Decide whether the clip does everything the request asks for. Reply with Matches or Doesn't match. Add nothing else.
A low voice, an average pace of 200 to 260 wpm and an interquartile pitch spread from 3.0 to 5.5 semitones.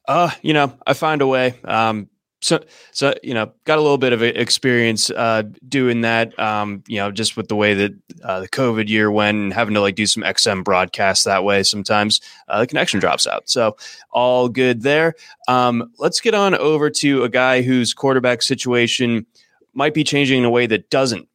Matches